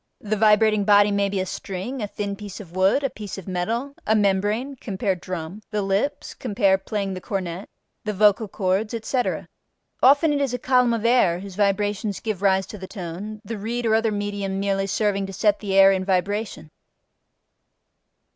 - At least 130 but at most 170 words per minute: No, average, 185 wpm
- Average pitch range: No, narrow, 2.2 semitones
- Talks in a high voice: Yes, high, 205 Hz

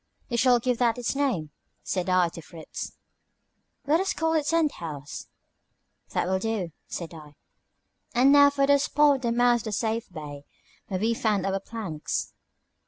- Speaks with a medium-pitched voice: No, high, 225 Hz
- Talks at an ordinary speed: Yes, average, 170 wpm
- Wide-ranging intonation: Yes, wide, 7.5 semitones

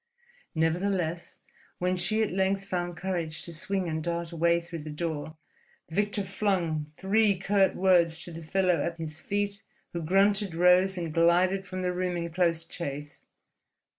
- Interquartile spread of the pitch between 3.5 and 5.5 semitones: No, narrow, 2.5 semitones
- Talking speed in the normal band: Yes, average, 160 wpm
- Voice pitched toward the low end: No, medium, 175 Hz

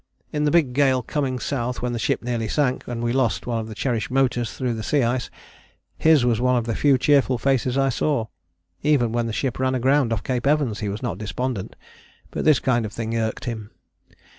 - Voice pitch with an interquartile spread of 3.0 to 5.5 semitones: No, narrow, 2.6 semitones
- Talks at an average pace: No, fast, 225 wpm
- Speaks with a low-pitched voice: Yes, low, 125 Hz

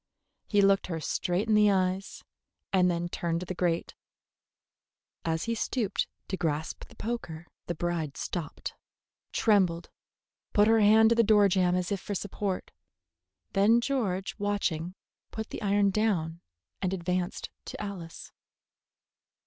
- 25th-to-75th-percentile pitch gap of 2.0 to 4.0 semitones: Yes, average, 3.1 semitones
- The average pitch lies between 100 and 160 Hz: No, high, 190 Hz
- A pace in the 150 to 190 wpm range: No, average, 140 wpm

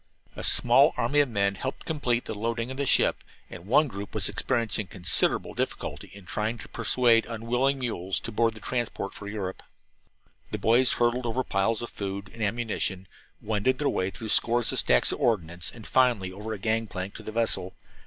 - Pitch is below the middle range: Yes, low, 115 Hz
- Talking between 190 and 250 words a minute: Yes, average, 195 wpm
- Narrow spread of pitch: No, average, 3.3 semitones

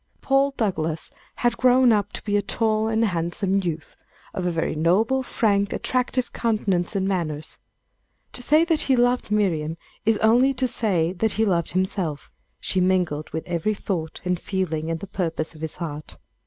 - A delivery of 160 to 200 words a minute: Yes, average, 170 wpm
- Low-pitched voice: No, high, 195 Hz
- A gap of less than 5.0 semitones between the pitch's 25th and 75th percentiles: No, average, 5.3 semitones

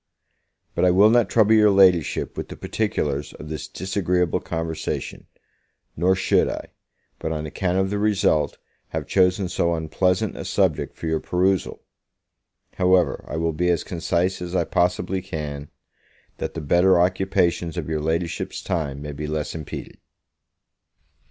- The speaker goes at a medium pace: Yes, average, 150 wpm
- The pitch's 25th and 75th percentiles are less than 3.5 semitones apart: Yes, average, 2.9 semitones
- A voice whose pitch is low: Yes, very low, 90 Hz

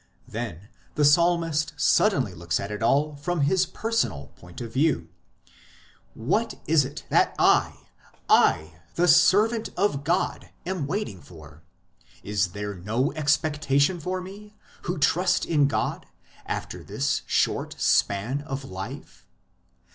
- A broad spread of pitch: Yes, wide, 8.9 semitones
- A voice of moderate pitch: Yes, medium, 145 Hz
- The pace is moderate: No, slow, 130 wpm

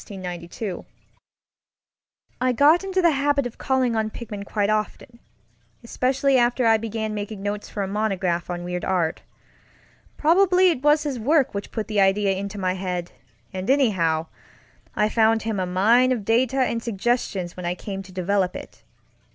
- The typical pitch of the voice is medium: No, high, 220 Hz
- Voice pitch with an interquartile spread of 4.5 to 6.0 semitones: Yes, average, 4.8 semitones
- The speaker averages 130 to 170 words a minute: Yes, average, 160 wpm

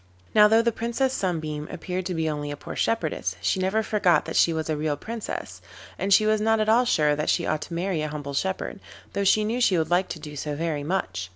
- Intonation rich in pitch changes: Yes, wide, 5.9 semitones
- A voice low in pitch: No, medium, 175 Hz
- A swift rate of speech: Yes, fast, 250 wpm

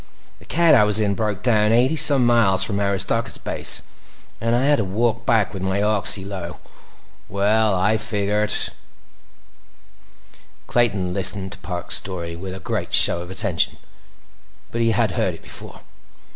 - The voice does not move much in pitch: No, average, 3.1 semitones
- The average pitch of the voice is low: Yes, low, 105 Hz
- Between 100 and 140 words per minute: No, average, 155 wpm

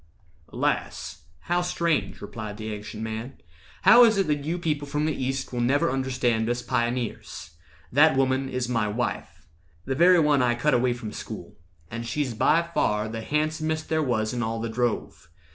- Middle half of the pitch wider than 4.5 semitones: Yes, average, 4.9 semitones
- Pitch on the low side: Yes, low, 125 Hz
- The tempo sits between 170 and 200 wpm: Yes, average, 175 wpm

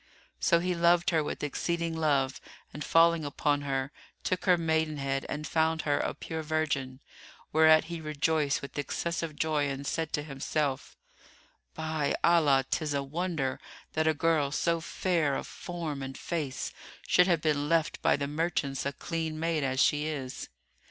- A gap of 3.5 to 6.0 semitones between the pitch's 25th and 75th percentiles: No, narrow, 2.6 semitones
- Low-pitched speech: No, medium, 155 Hz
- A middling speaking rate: Yes, average, 165 wpm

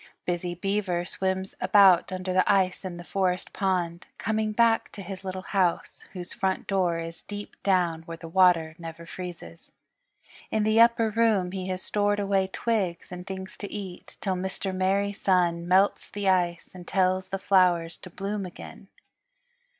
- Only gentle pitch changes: Yes, narrow, 2.0 semitones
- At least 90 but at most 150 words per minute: No, average, 165 wpm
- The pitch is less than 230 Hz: Yes, medium, 185 Hz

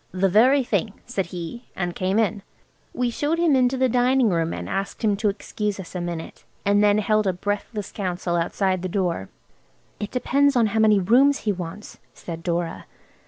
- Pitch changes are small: No, average, 4.8 semitones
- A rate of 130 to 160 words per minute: No, average, 185 wpm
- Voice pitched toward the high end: Yes, high, 205 Hz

